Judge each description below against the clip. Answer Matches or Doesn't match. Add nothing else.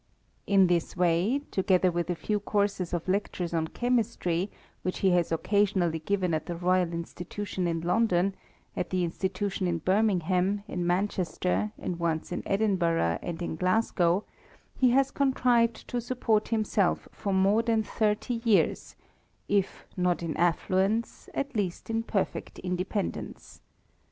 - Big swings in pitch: Doesn't match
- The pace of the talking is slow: Doesn't match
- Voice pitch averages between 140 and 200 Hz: Matches